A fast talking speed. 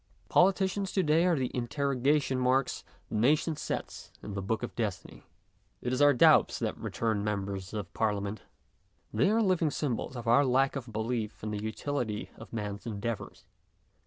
No: average, 165 wpm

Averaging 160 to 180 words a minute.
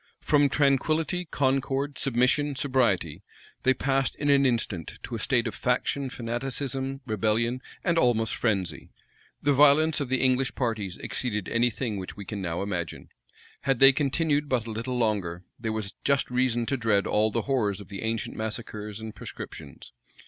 Yes: average, 165 wpm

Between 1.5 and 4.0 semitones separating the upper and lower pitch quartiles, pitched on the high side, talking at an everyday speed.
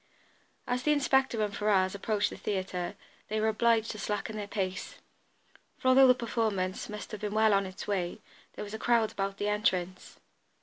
Yes: narrow, 2.4 semitones; high, 210 Hz; average, 185 wpm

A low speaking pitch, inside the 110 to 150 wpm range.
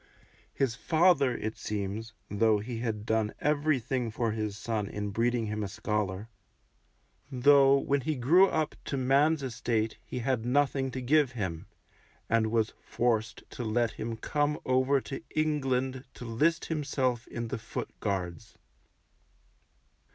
Yes: low, 120 Hz; average, 145 wpm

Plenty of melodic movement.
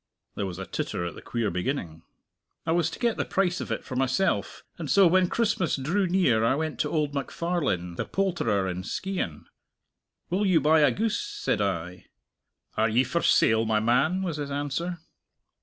Yes: wide, 8.5 semitones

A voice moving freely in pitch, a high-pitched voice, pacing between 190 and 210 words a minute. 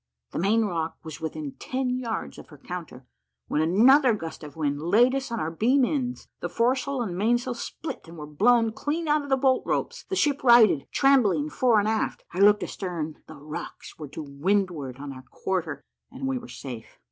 Yes: wide, 8.3 semitones; high, 210 Hz; average, 200 wpm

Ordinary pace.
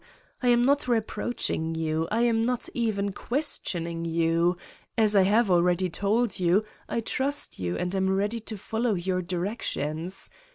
Yes: average, 155 wpm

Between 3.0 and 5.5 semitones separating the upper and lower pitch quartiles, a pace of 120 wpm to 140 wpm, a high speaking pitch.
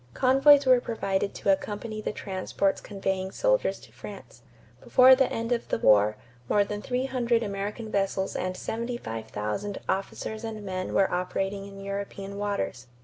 No: average, 3.3 semitones; average, 150 wpm; high, 200 Hz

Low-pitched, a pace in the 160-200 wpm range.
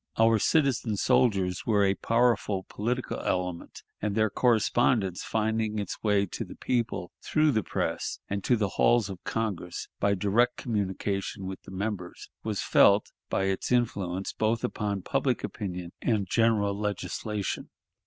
No: low, 105 Hz; average, 145 wpm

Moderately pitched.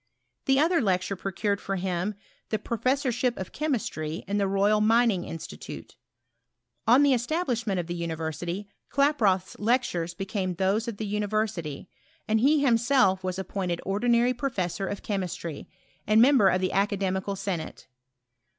No: high, 200 Hz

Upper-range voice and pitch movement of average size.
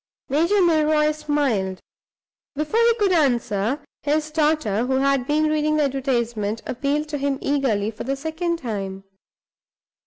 Yes: very high, 285 Hz; average, 4.4 semitones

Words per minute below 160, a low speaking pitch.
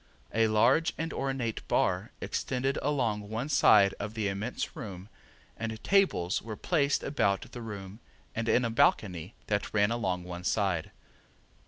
Yes: average, 150 wpm; low, 110 Hz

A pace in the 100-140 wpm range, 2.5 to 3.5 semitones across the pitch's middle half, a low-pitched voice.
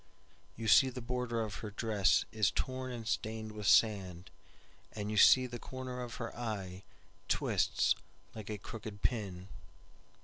Yes: slow, 135 wpm; average, 2.9 semitones; low, 110 Hz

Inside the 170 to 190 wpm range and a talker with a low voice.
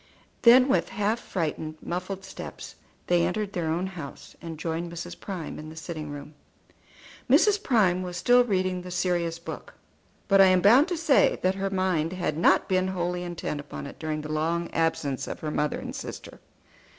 No: average, 185 wpm; medium, 175 Hz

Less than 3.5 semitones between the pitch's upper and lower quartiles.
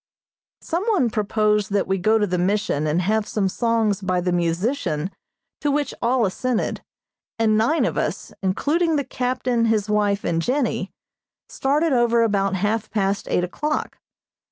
No: average, 4.6 semitones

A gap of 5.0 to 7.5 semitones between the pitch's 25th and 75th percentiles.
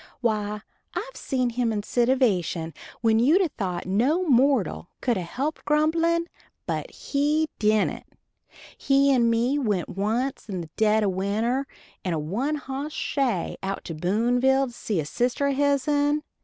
Yes: average, 5.3 semitones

